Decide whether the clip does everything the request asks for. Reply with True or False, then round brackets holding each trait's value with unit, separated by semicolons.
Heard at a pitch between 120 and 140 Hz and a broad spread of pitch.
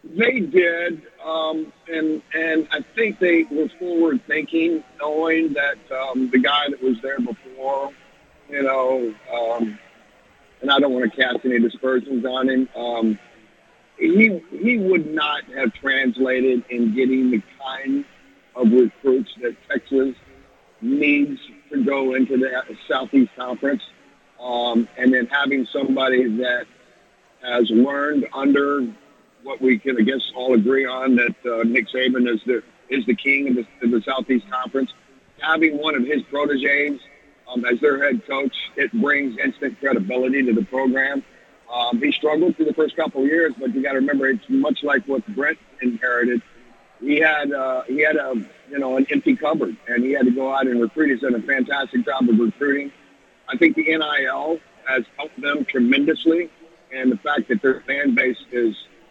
False (135 Hz; 3.9 semitones)